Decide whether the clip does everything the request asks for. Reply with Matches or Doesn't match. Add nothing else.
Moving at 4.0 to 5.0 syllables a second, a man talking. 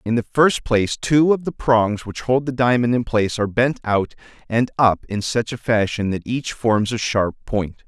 Matches